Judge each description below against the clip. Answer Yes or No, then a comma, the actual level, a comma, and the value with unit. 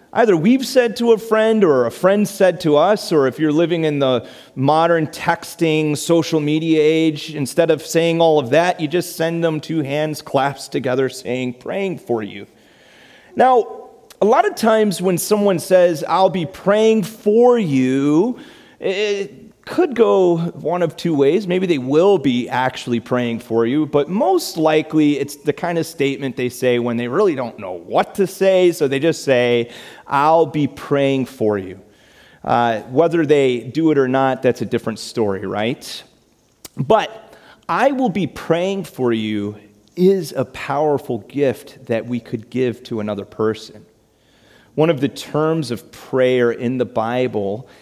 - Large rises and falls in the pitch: Yes, wide, 6.0 semitones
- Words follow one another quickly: No, average, 170 wpm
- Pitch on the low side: No, medium, 150 Hz